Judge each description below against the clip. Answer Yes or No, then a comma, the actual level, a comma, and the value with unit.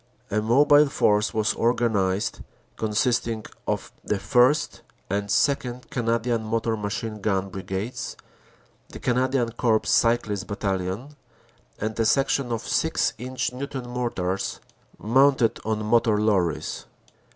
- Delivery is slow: Yes, slow, 115 wpm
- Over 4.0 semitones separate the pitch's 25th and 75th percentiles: No, average, 3.1 semitones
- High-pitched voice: No, low, 115 Hz